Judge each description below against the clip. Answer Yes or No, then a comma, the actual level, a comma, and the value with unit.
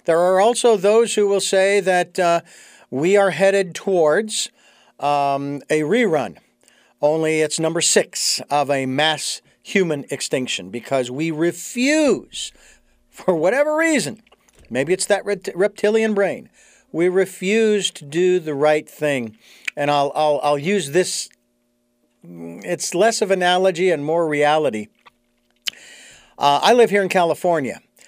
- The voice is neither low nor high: Yes, medium, 170 Hz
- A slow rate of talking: Yes, slow, 130 wpm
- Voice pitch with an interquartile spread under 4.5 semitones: No, wide, 5.5 semitones